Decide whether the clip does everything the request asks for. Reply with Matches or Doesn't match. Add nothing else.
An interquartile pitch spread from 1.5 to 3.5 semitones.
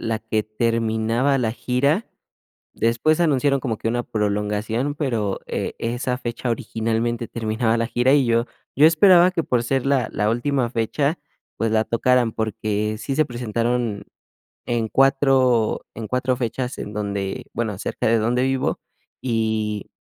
Matches